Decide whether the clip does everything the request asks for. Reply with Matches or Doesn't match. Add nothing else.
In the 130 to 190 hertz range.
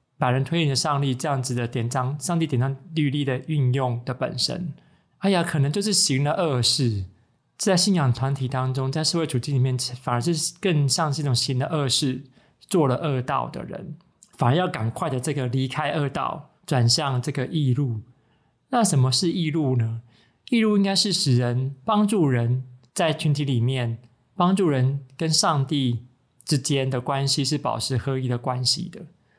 Matches